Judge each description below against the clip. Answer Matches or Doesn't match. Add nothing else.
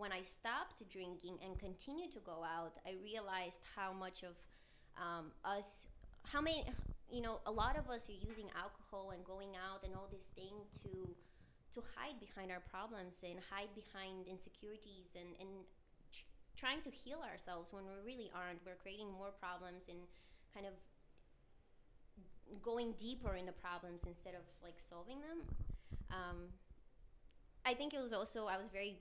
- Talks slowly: Doesn't match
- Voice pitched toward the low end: Doesn't match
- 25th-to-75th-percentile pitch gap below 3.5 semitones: Matches